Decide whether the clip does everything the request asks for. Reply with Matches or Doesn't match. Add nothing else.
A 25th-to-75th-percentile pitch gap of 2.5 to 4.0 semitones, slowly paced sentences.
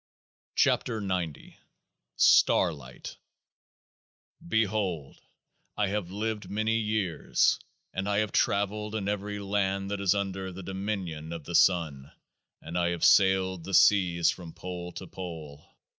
Matches